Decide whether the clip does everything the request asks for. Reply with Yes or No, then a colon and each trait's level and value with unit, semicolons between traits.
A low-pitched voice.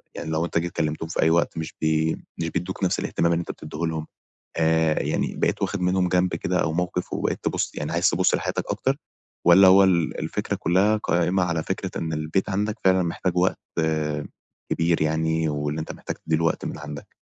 Yes: very low, 85 Hz